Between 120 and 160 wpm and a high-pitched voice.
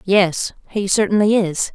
Yes: average, 140 wpm; high, 195 Hz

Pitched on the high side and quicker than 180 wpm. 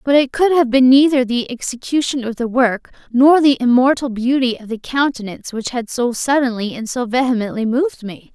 Yes: very high, 250 Hz; average, 195 wpm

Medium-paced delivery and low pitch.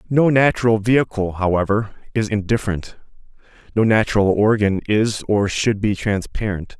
No: slow, 125 wpm; low, 105 Hz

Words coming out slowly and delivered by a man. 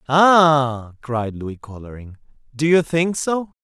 Yes: slow, 130 wpm; male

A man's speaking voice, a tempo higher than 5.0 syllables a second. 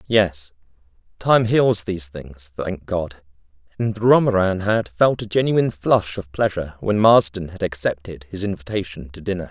No: male; 4.7 syllables/s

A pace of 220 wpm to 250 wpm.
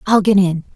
Yes: fast, 240 wpm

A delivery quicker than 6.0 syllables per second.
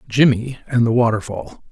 No: 5.0 syllables/s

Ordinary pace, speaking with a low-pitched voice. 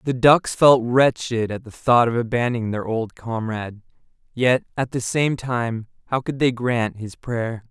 Yes: average, 180 wpm; low, 120 Hz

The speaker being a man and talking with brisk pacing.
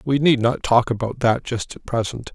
Yes: male; fast, 230 wpm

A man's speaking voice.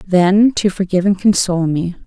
No: female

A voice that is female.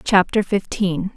Yes: female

